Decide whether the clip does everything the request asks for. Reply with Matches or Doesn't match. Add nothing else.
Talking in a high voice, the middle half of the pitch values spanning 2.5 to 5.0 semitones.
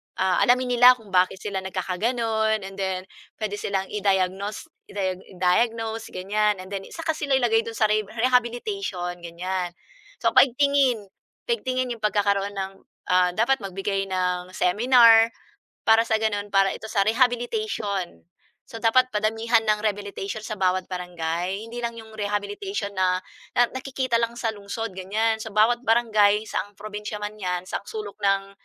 Matches